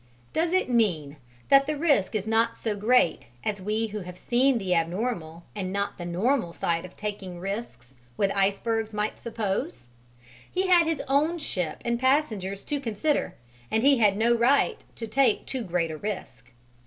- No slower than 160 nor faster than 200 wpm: Yes, average, 175 wpm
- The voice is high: Yes, high, 215 Hz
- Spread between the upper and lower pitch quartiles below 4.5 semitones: No, wide, 5.5 semitones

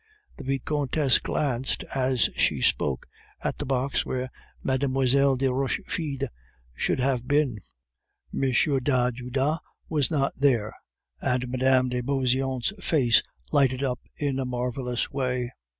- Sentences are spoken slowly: Yes, slow, 120 wpm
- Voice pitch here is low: Yes, low, 130 Hz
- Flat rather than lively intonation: Yes, narrow, 1.6 semitones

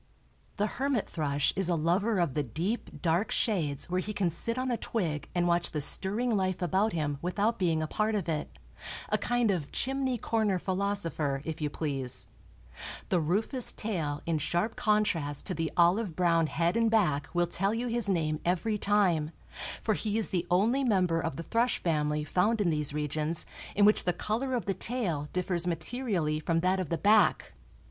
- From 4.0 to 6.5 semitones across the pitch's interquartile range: Yes, average, 5.1 semitones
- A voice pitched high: No, medium, 180 Hz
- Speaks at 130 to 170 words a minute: No, average, 185 wpm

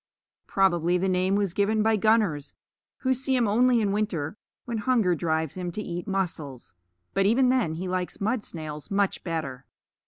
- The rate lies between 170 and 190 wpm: Yes, average, 175 wpm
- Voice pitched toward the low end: No, high, 195 Hz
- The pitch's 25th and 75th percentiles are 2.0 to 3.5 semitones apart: No, average, 4.4 semitones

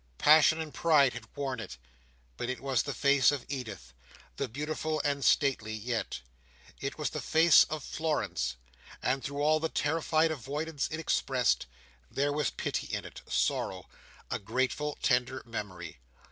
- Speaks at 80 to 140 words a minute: No, average, 155 wpm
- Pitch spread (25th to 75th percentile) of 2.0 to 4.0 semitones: Yes, average, 3.5 semitones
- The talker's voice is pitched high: No, medium, 140 Hz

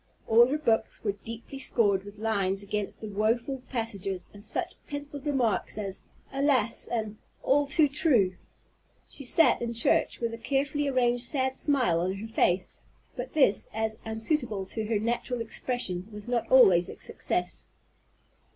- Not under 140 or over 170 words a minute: Yes, average, 155 wpm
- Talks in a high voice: Yes, high, 230 Hz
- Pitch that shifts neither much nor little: Yes, average, 4.3 semitones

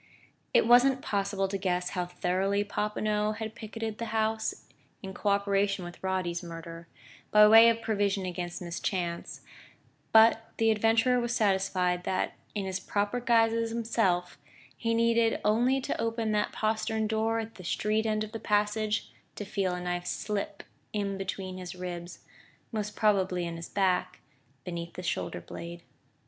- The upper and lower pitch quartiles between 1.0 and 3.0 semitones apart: No, average, 3.5 semitones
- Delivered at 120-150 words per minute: No, average, 160 wpm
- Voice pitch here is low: No, high, 205 Hz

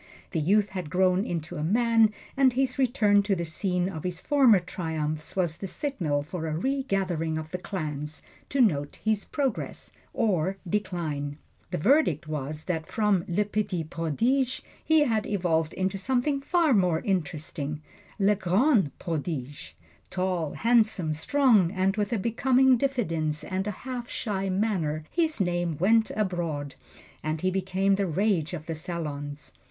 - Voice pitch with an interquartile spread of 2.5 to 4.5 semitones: No, wide, 5.5 semitones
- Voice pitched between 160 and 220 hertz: Yes, medium, 185 Hz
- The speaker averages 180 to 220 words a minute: No, average, 155 wpm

